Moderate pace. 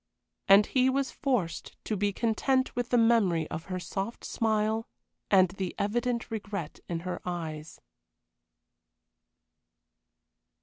No: slow, 120 wpm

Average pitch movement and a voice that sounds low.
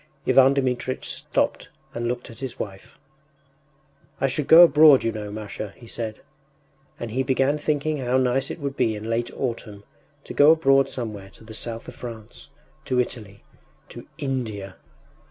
Yes: average, 3.7 semitones; low, 125 Hz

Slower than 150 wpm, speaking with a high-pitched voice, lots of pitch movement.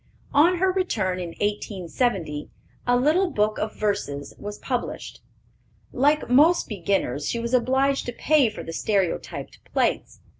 Yes: average, 140 wpm; high, 230 Hz; wide, 6.1 semitones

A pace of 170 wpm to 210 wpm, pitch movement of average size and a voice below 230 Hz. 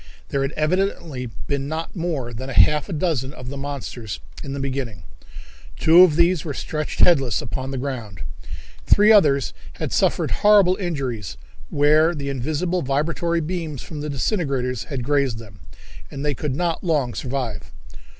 No: average, 160 wpm; average, 4.1 semitones; medium, 140 Hz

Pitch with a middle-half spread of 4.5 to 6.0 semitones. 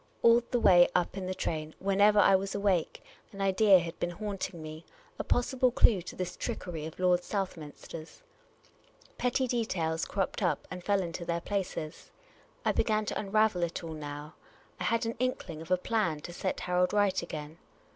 No: average, 3.6 semitones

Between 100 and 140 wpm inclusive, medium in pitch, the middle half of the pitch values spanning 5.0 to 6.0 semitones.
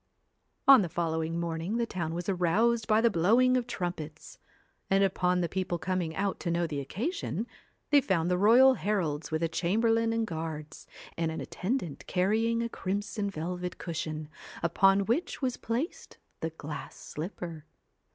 No: average, 160 wpm; medium, 180 Hz; wide, 5.4 semitones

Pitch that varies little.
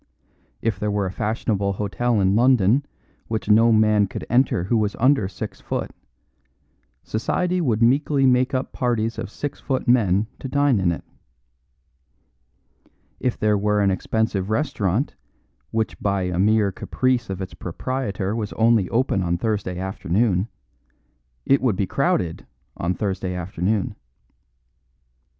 No: average, 4.1 semitones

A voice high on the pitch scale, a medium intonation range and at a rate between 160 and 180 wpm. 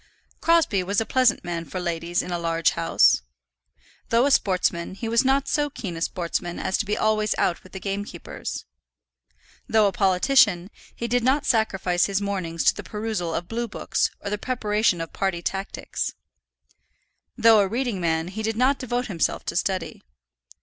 Yes: high, 200 Hz; average, 4.7 semitones; average, 175 wpm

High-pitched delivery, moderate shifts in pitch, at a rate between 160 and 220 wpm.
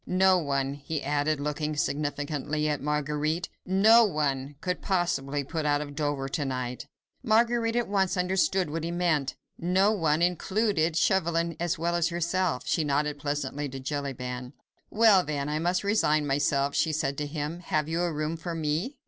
No: medium, 155 Hz; average, 3.6 semitones; average, 170 wpm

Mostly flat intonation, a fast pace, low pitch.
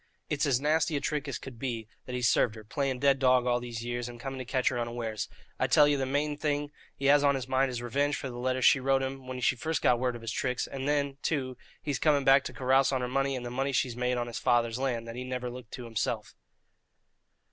Yes: narrow, 2.3 semitones; fast, 265 wpm; low, 130 Hz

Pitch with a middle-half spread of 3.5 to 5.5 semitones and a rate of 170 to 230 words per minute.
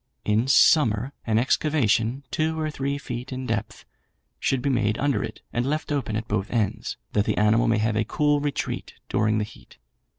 Yes: average, 4.6 semitones; average, 190 wpm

